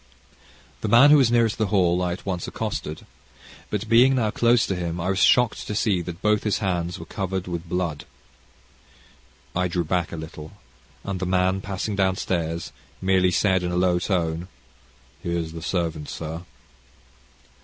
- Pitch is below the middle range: Yes, very low, 90 Hz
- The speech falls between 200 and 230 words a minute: No, average, 170 wpm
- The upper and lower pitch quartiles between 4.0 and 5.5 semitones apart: No, average, 2.8 semitones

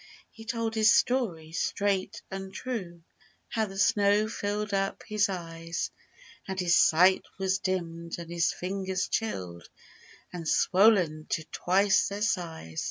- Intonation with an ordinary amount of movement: Yes, average, 3.5 semitones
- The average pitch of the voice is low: No, high, 190 Hz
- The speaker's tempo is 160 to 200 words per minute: No, slow, 135 wpm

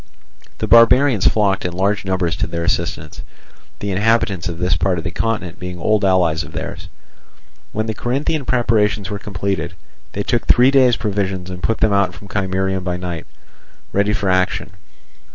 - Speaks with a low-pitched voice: Yes, low, 100 Hz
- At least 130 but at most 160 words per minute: No, average, 170 wpm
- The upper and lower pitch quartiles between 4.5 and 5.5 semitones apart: No, average, 3.2 semitones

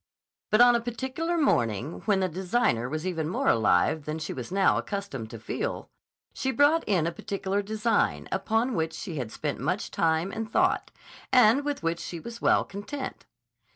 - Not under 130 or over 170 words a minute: No, average, 180 wpm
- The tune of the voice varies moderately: No, wide, 6.8 semitones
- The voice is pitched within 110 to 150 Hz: No, high, 195 Hz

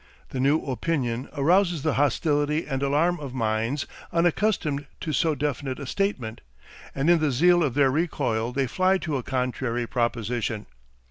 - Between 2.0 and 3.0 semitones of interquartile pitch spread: No, average, 4.2 semitones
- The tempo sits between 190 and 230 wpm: No, average, 155 wpm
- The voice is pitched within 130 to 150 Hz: Yes, medium, 140 Hz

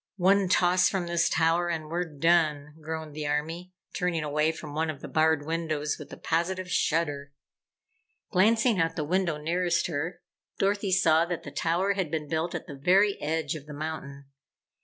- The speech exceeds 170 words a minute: Yes, average, 180 wpm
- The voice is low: No, medium, 165 Hz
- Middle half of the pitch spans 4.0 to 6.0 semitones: No, average, 2.8 semitones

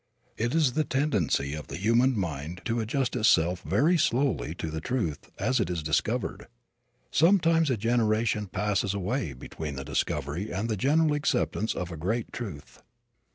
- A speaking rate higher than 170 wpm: No, average, 160 wpm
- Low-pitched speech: Yes, low, 110 Hz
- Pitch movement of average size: No, wide, 7.5 semitones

